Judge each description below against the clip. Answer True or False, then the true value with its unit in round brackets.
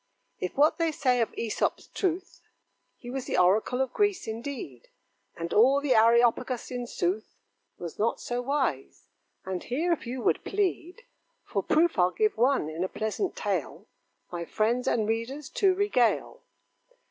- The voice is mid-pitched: False (245 Hz)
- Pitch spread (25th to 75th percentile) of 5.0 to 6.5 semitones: True (5.4 semitones)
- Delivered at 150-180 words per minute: True (160 wpm)